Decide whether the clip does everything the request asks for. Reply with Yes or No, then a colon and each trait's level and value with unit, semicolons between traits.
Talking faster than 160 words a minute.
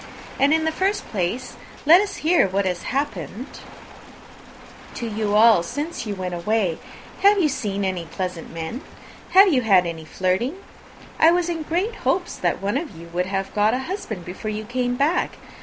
Yes: average, 180 wpm